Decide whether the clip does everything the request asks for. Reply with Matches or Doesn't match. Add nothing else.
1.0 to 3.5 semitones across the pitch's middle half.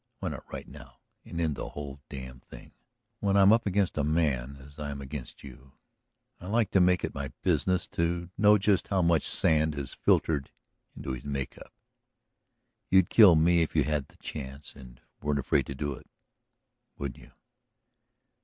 Doesn't match